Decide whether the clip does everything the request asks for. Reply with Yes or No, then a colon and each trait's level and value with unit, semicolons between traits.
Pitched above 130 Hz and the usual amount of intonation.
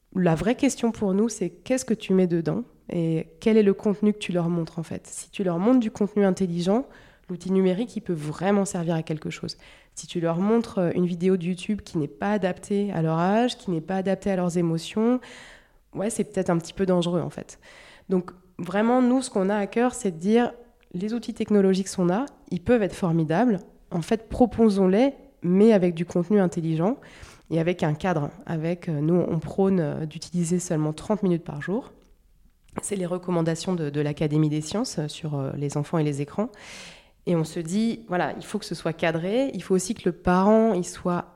Yes: medium, 185 Hz; average, 3.8 semitones